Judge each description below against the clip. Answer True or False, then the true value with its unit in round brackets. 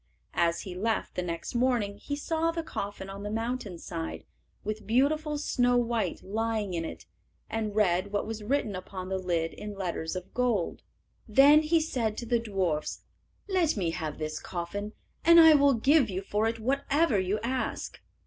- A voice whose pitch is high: True (215 Hz)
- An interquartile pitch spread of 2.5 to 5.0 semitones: False (5.5 semitones)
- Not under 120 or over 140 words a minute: False (175 wpm)